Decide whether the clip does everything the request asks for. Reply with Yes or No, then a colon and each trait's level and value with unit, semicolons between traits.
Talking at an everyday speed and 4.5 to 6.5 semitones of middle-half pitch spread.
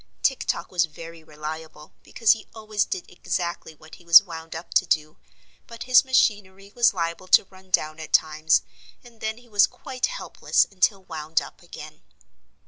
Yes: average, 175 wpm; average, 5.1 semitones